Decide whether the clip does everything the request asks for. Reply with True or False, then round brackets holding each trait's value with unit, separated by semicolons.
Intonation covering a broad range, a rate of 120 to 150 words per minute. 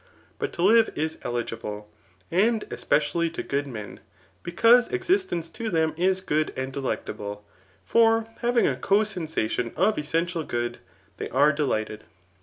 True (8.6 semitones; 140 wpm)